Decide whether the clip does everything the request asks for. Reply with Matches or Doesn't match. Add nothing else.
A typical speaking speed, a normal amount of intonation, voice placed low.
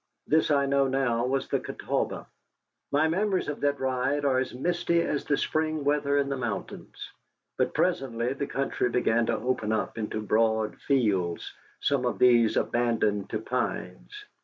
Matches